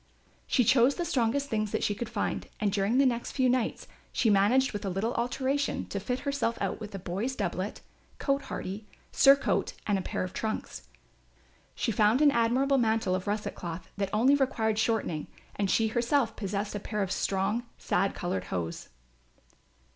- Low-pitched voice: No, high, 220 Hz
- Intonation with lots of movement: No, average, 4.1 semitones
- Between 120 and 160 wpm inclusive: No, average, 180 wpm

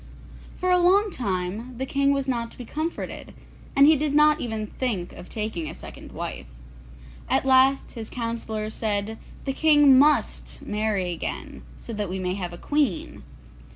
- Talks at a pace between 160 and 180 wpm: Yes, average, 170 wpm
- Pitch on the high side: Yes, high, 240 Hz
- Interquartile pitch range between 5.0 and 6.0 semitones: Yes, wide, 5.5 semitones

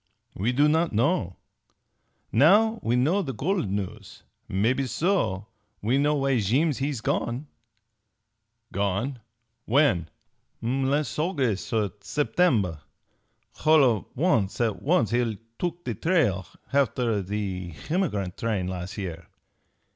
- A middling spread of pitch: No, wide, 7.1 semitones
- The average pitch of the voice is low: Yes, low, 125 Hz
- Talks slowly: Yes, slow, 115 wpm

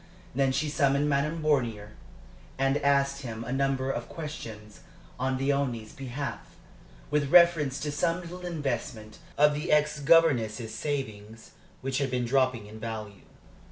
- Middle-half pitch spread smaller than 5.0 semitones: Yes, average, 4.0 semitones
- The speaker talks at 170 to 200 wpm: No, average, 140 wpm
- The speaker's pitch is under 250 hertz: Yes, low, 135 Hz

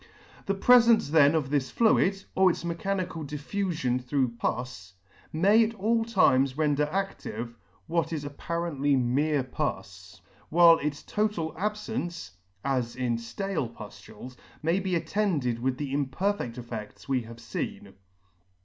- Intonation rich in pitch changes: Yes, wide, 7.0 semitones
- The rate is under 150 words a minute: Yes, average, 140 wpm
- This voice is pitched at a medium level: Yes, medium, 150 Hz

